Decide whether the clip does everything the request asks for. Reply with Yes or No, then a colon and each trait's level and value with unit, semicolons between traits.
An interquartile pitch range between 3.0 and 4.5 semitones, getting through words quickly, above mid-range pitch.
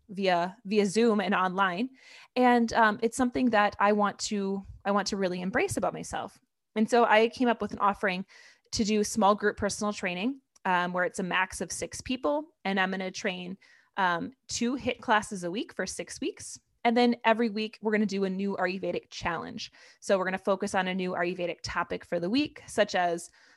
Yes: average, 3.5 semitones; fast, 210 wpm; high, 205 Hz